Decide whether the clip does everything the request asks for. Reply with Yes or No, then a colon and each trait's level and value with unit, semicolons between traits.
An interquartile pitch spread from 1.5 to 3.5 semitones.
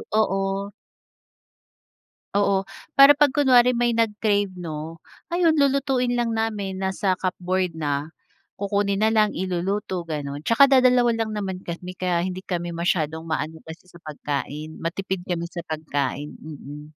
No: average, 5.3 semitones